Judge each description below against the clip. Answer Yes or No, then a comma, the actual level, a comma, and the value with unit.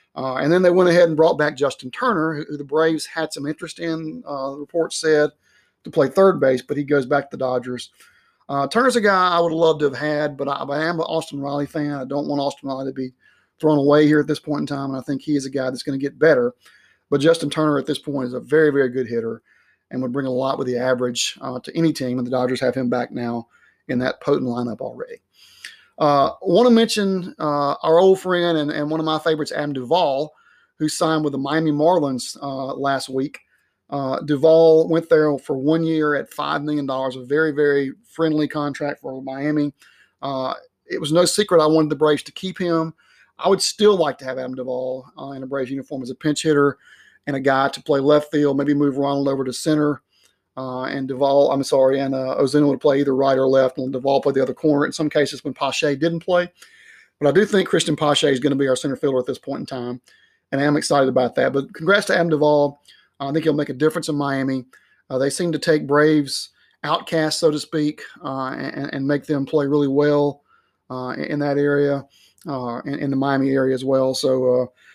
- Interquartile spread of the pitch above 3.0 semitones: No, narrow, 2.6 semitones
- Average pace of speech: No, fast, 235 wpm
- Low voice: No, medium, 145 Hz